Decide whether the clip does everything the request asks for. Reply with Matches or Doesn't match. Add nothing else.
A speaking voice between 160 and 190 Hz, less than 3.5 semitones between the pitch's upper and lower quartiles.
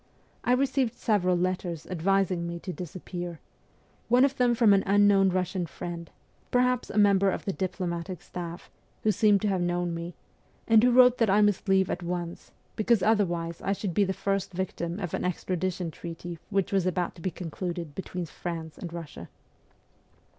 Matches